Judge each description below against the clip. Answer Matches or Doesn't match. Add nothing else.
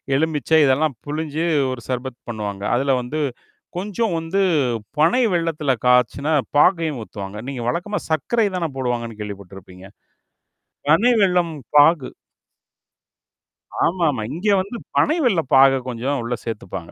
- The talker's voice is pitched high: Doesn't match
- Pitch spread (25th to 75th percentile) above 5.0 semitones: Matches